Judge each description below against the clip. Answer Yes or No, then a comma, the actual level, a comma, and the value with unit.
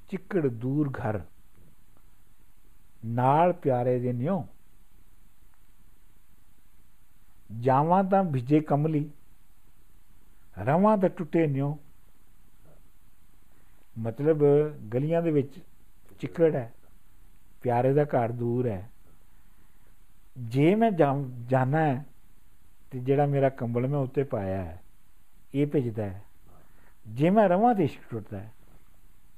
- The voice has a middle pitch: No, low, 120 Hz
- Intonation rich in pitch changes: Yes, wide, 7.6 semitones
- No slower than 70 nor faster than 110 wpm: Yes, slow, 95 wpm